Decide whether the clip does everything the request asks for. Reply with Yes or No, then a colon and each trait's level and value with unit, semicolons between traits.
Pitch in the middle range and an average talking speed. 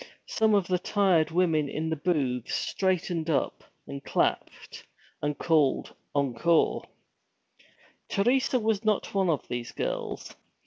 No: medium, 170 Hz; slow, 125 wpm